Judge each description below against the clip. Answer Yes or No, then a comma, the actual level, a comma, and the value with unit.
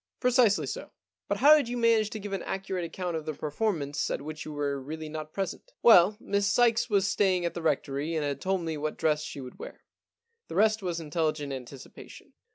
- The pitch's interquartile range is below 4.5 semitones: No, wide, 5.4 semitones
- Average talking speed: No, fast, 230 wpm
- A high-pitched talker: No, medium, 170 Hz